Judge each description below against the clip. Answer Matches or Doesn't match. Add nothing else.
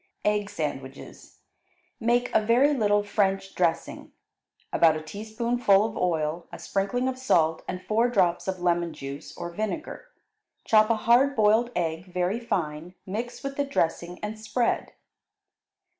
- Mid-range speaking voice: Doesn't match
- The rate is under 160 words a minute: Matches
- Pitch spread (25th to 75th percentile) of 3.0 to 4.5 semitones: Doesn't match